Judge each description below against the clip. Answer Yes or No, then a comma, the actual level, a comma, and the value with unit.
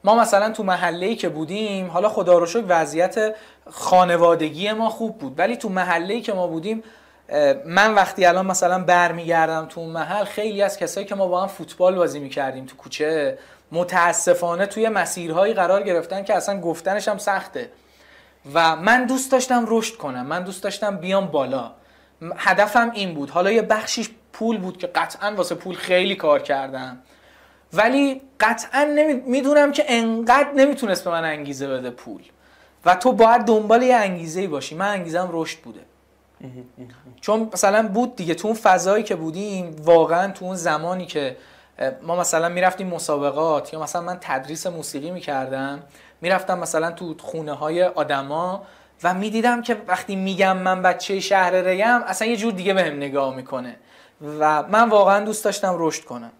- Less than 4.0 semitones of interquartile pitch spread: No, average, 4.7 semitones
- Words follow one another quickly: Yes, fast, 165 wpm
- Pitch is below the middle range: No, medium, 185 Hz